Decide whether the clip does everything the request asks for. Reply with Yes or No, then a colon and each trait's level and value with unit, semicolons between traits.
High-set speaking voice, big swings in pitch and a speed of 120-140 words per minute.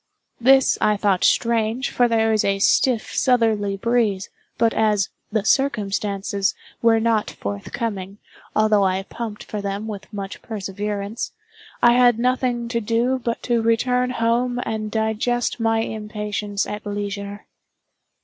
No: high, 220 Hz; narrow, 2.5 semitones; slow, 135 wpm